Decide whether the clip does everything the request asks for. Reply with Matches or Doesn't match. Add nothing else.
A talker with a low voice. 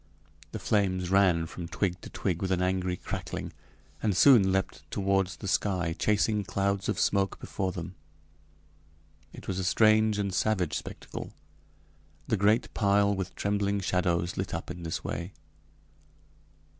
Matches